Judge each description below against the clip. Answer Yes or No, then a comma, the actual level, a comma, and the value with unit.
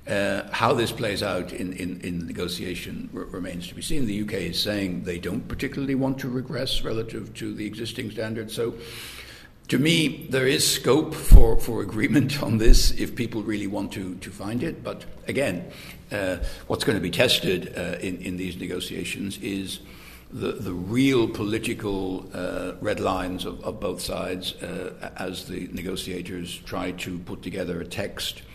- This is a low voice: Yes, low, 100 Hz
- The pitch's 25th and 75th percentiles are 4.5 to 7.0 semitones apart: No, average, 4.1 semitones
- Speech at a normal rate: Yes, average, 175 wpm